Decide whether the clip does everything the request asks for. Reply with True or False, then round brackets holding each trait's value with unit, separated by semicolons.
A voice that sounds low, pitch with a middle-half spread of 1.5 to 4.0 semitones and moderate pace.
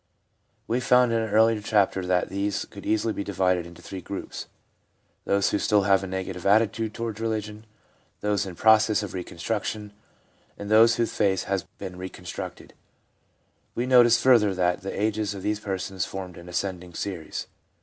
True (100 Hz; 2.8 semitones; 170 wpm)